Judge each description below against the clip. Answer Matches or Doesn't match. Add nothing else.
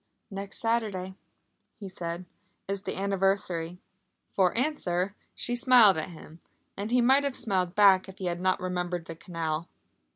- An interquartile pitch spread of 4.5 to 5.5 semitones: Doesn't match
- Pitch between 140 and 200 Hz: Matches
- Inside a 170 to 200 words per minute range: Doesn't match